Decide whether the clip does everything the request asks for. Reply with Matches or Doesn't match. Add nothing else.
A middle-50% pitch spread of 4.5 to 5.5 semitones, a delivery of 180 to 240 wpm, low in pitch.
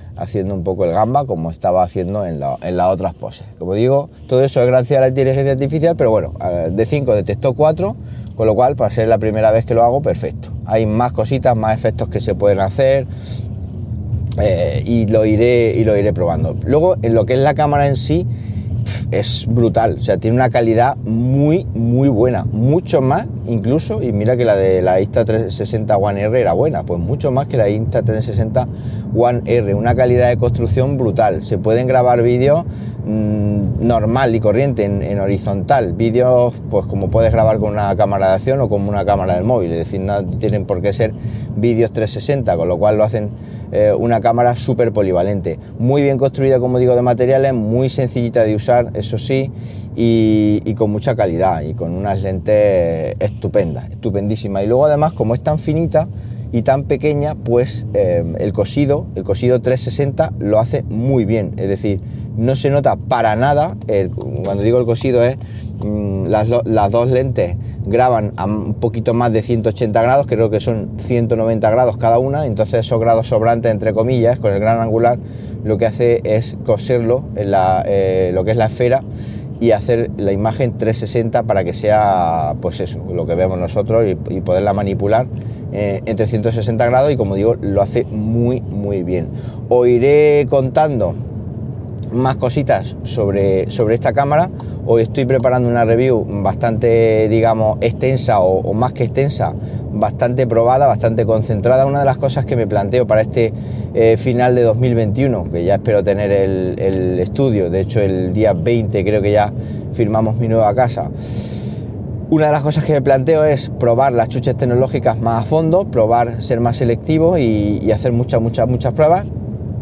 Doesn't match